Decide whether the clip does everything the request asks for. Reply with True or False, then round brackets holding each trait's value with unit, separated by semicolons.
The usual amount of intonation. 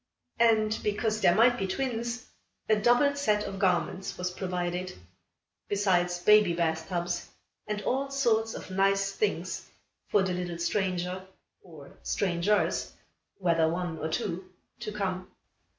True (3.4 semitones)